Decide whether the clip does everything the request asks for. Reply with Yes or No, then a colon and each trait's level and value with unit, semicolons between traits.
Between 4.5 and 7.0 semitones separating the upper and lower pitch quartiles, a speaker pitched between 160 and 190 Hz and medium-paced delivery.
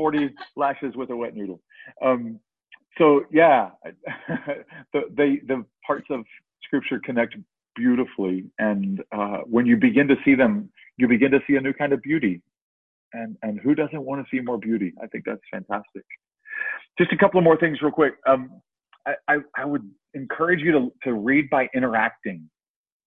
No: average, 5.1 semitones; low, 135 Hz; average, 175 wpm